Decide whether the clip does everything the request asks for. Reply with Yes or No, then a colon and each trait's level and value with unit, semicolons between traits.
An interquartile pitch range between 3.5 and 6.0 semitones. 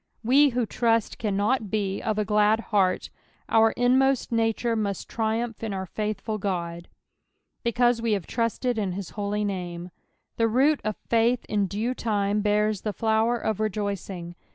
No: narrow, 2.4 semitones